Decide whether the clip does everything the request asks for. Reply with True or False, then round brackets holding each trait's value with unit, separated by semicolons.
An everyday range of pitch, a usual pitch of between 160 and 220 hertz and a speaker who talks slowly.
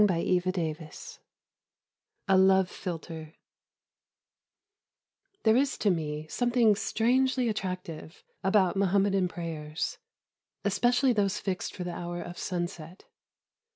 True (3.3 semitones; 185 Hz; 95 wpm)